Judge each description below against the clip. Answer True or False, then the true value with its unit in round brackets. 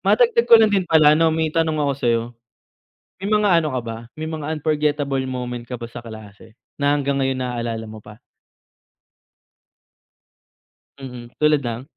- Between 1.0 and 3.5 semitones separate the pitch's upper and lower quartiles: False (4.9 semitones)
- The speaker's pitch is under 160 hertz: True (140 Hz)